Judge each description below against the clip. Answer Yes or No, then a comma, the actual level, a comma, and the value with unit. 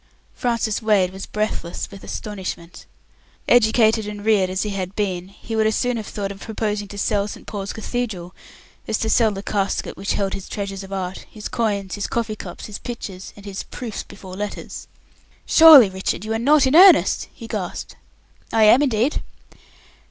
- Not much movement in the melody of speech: Yes, narrow, 2.3 semitones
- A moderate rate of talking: Yes, average, 180 wpm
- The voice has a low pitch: No, high, 210 Hz